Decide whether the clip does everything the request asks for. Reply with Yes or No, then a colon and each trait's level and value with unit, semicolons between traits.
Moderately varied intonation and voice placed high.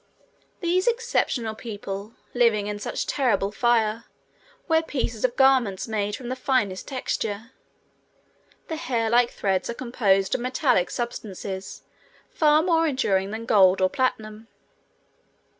Yes: average, 4.1 semitones; high, 230 Hz